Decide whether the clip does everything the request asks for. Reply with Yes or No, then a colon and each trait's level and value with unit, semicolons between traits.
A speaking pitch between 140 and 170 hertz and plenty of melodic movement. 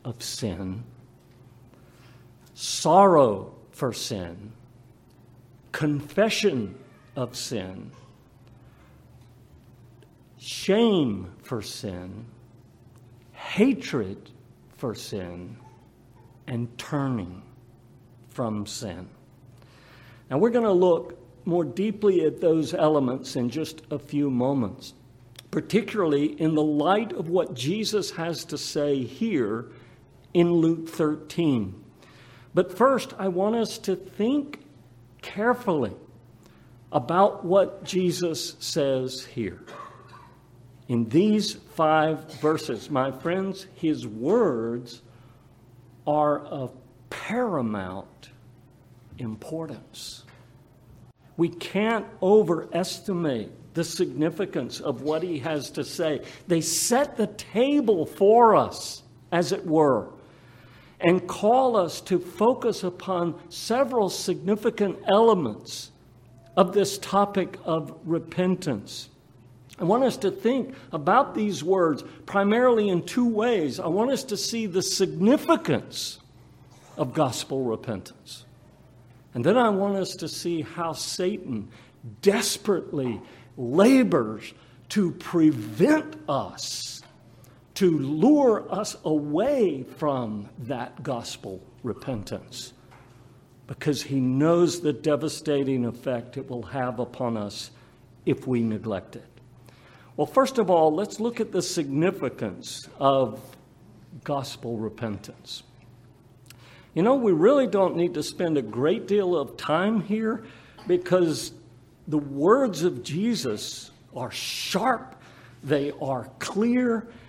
Yes: medium, 150 Hz; wide, 7.0 semitones